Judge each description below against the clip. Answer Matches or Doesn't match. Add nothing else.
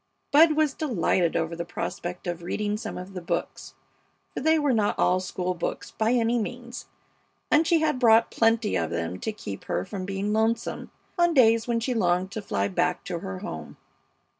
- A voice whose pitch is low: Doesn't match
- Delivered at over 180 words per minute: Matches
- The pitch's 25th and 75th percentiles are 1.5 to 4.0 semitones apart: Doesn't match